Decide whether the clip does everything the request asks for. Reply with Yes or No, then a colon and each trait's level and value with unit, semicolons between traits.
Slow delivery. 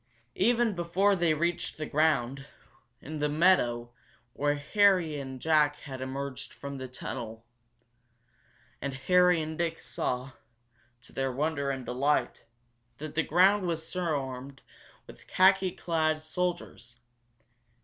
Yes: slow, 120 wpm